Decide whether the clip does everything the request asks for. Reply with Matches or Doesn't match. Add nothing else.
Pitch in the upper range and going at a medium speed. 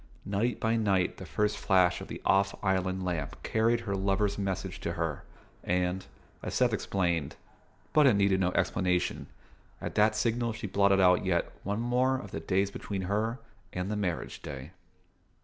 Doesn't match